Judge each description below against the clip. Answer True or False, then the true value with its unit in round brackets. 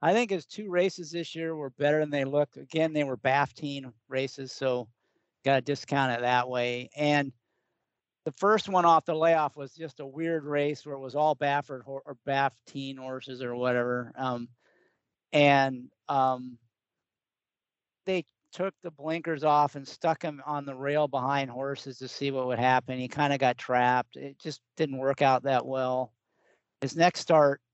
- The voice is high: False (140 Hz)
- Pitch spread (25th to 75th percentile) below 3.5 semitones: True (2.9 semitones)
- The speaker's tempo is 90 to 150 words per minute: False (180 wpm)